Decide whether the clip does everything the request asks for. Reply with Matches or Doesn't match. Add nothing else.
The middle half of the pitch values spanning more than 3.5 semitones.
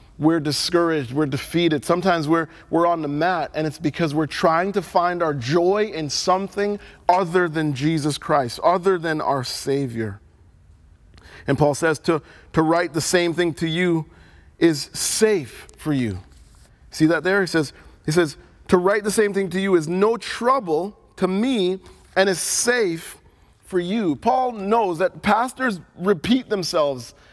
Matches